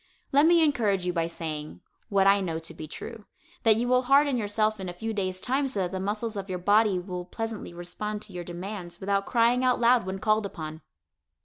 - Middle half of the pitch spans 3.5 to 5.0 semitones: Yes, average, 4.1 semitones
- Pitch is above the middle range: Yes, high, 200 Hz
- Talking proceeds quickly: Yes, fast, 220 wpm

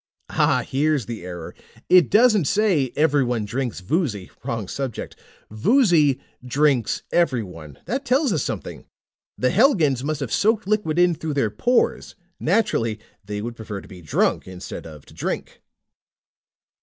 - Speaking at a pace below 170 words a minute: Yes, average, 145 wpm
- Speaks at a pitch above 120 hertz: Yes, medium, 140 Hz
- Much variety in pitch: Yes, wide, 8.9 semitones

